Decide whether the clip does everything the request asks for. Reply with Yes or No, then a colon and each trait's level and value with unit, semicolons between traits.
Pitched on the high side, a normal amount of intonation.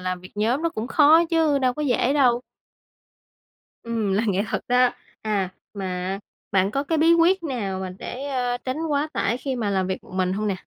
No: high, 245 Hz; wide, 6.6 semitones